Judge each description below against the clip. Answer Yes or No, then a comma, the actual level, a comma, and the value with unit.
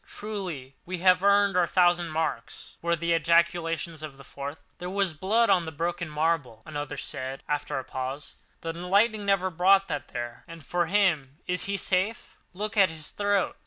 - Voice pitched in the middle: Yes, medium, 170 Hz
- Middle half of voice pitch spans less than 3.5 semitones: No, average, 3.8 semitones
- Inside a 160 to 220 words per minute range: Yes, average, 170 wpm